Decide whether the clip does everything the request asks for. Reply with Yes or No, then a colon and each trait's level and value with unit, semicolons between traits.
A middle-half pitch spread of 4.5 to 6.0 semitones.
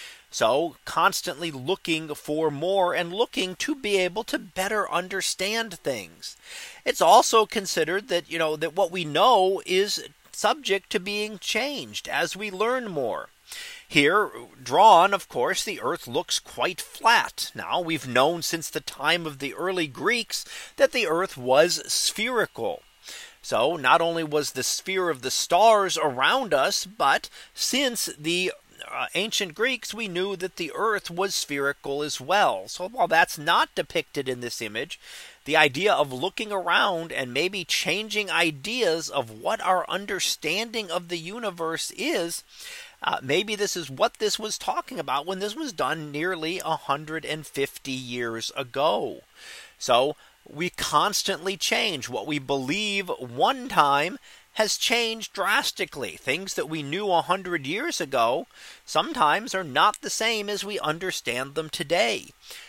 Yes: average, 5.2 semitones